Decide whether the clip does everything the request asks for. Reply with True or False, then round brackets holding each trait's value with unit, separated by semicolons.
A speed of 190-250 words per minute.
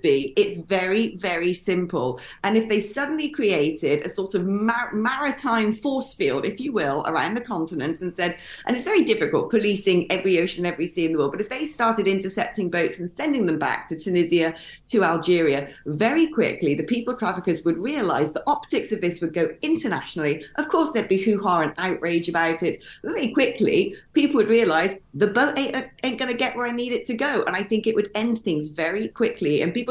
True (205 wpm)